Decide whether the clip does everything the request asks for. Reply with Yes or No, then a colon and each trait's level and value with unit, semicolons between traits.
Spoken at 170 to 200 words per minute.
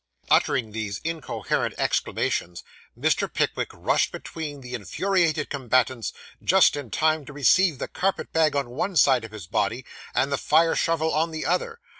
No: average, 160 wpm